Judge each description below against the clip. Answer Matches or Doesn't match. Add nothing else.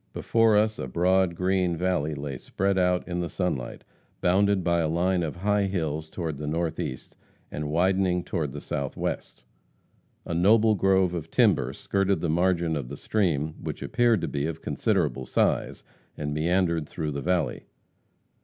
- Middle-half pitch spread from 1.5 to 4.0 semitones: Matches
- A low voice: Matches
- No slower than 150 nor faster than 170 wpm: Matches